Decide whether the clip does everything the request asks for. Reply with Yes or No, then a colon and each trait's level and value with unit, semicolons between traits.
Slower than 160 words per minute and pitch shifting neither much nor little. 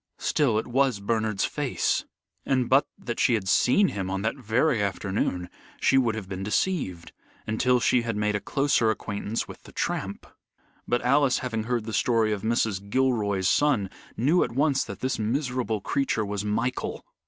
No: average, 175 wpm; average, 3.9 semitones